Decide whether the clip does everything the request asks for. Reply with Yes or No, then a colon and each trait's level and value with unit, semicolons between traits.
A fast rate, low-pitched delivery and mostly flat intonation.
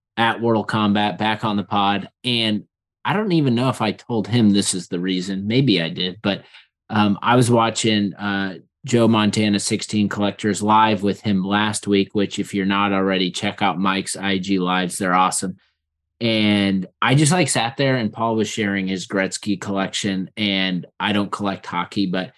No: average, 185 wpm; low, 100 Hz; narrow, 2.3 semitones